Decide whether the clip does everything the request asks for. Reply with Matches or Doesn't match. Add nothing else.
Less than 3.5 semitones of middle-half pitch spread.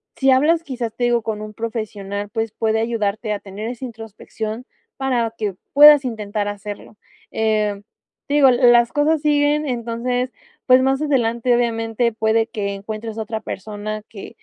Matches